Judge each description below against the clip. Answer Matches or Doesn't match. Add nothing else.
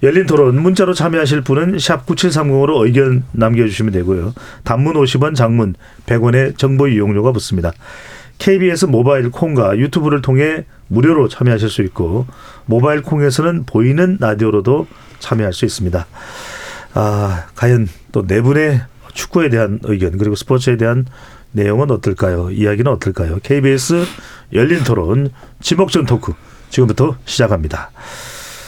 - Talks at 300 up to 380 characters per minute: Matches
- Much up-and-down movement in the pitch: Doesn't match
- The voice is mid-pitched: Doesn't match